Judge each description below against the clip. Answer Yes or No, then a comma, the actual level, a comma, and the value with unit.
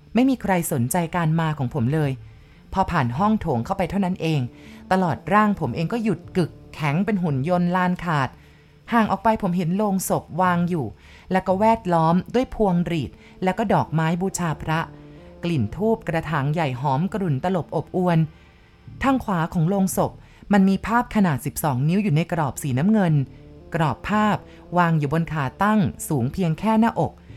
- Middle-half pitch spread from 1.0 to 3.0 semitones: No, average, 4.6 semitones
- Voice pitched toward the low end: No, medium, 170 Hz